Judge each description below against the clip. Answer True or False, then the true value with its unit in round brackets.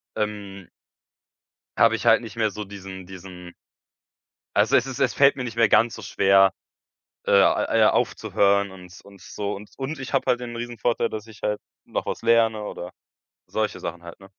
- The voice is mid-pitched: False (105 Hz)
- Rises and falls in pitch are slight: False (3.2 semitones)